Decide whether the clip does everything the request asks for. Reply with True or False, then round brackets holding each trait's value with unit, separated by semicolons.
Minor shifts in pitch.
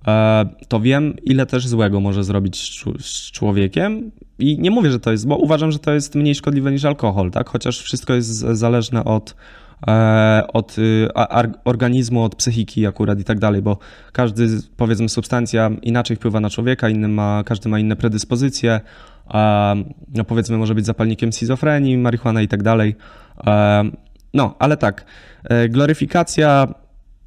False (3.1 semitones)